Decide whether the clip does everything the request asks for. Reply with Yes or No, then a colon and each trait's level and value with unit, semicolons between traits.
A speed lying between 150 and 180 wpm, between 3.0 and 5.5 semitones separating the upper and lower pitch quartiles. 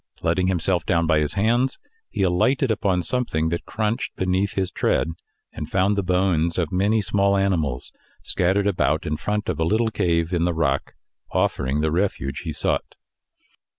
Yes: average, 170 wpm; average, 3.8 semitones